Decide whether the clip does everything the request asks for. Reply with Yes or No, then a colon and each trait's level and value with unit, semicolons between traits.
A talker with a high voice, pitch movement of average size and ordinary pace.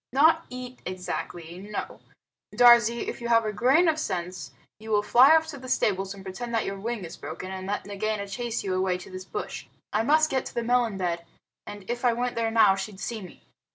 No: high, 215 Hz; average, 4.3 semitones; fast, 225 wpm